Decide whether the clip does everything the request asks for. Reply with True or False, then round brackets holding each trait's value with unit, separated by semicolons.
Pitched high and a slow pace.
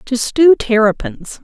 True (235 Hz; 125 wpm)